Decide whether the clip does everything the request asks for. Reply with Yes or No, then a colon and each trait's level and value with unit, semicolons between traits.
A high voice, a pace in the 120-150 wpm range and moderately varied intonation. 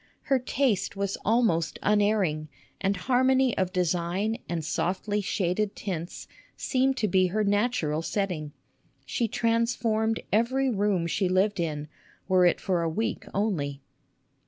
Yes: high, 200 Hz; slow, 135 wpm; average, 4.3 semitones